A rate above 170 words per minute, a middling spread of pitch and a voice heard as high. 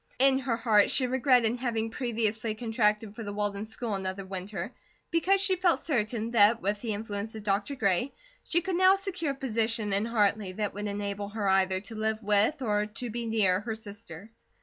Yes: average, 195 wpm; average, 3.1 semitones; high, 220 Hz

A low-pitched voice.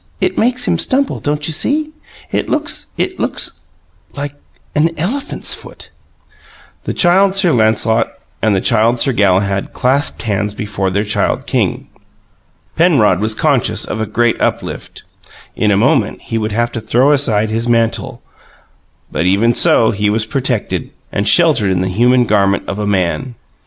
Yes: low, 115 Hz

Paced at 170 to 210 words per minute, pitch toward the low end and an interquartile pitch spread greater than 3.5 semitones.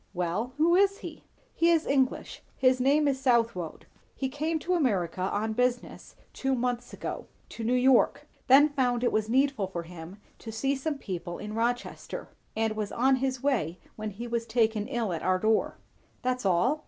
No: average, 180 wpm; high, 245 Hz; average, 4.0 semitones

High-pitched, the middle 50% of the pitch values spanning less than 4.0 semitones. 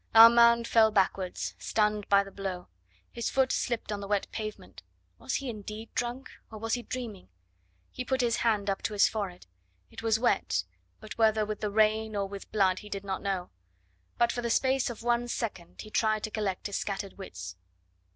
Yes: high, 215 Hz; average, 2.8 semitones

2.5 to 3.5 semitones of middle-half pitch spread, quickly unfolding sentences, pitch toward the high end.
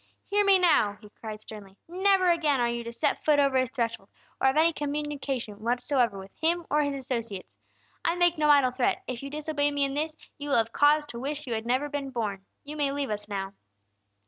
No: average, 4.4 semitones; fast, 225 wpm; very high, 275 Hz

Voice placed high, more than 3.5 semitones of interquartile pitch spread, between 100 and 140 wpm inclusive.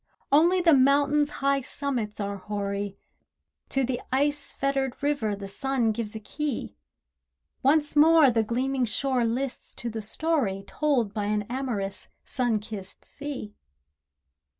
Yes: very high, 255 Hz; average, 5.1 semitones; slow, 135 wpm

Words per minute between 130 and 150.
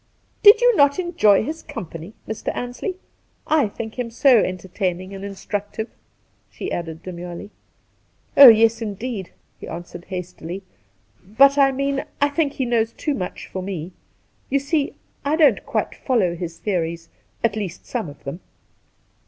No: average, 165 wpm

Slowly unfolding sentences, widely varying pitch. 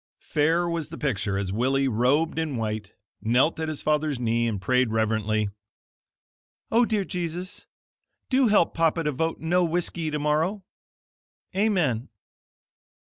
Yes: slow, 130 wpm; wide, 6.3 semitones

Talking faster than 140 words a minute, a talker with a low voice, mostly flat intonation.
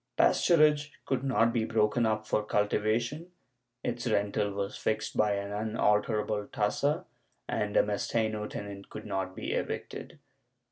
No: slow, 135 wpm; low, 110 Hz; narrow, 2.3 semitones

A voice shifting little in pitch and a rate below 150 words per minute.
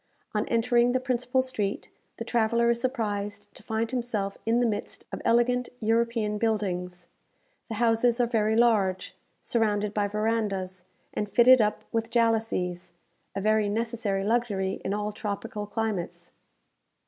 Yes: narrow, 2.3 semitones; average, 140 wpm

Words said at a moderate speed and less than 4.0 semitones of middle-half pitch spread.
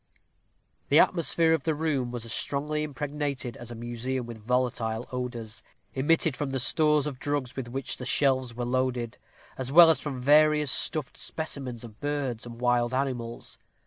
Yes: average, 170 wpm; average, 3.4 semitones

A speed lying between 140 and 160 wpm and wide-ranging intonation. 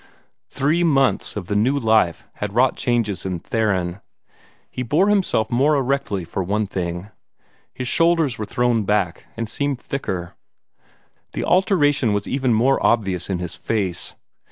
Yes: average, 150 wpm; wide, 6.0 semitones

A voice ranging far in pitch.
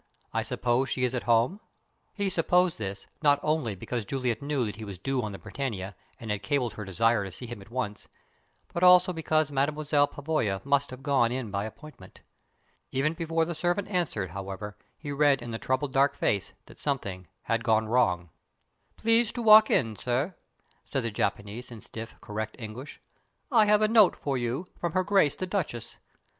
Yes: wide, 6.2 semitones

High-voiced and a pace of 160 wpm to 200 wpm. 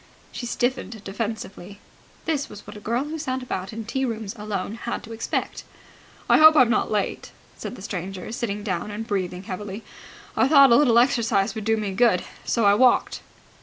Yes: high, 220 Hz; average, 185 wpm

